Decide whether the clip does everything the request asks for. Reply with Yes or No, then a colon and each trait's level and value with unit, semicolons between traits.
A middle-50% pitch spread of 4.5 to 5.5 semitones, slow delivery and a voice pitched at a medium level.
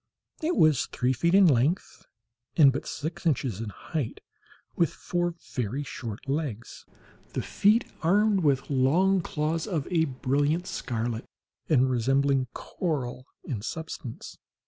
Yes: average, 4.8 semitones; slow, 130 wpm; medium, 145 Hz